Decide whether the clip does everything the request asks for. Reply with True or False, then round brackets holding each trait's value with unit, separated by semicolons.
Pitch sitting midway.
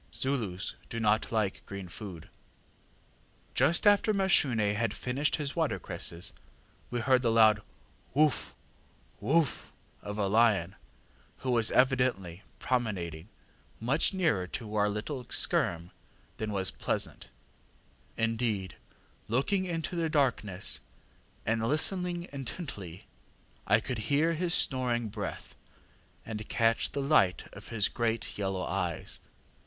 False (115 Hz)